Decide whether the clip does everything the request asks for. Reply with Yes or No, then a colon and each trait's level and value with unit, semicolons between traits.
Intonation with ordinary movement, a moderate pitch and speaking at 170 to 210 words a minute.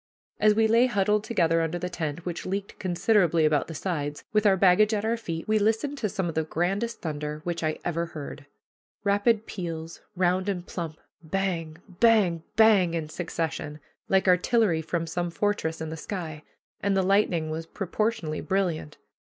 Yes: average, 4.1 semitones; medium, 175 Hz; average, 175 wpm